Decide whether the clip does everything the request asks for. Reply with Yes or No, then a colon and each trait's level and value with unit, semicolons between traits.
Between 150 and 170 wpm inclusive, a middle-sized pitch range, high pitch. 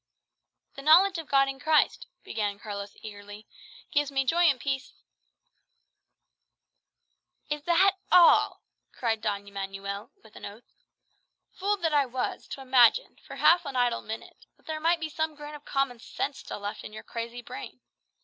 No: average, 165 wpm; wide, 6.3 semitones; very high, 270 Hz